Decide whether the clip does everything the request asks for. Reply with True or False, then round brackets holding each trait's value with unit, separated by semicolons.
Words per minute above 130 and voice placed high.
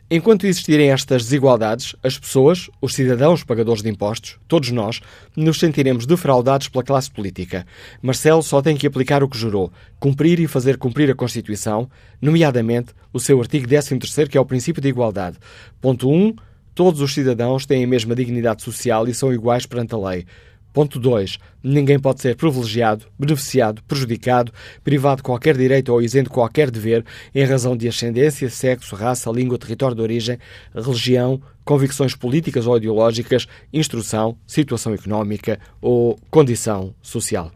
False (160 wpm; 125 Hz)